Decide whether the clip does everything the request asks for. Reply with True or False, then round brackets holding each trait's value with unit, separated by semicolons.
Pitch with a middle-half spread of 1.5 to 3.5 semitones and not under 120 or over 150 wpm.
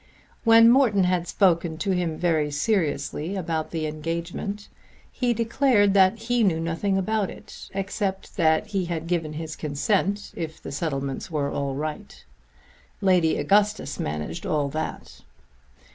False (4.4 semitones; 140 wpm)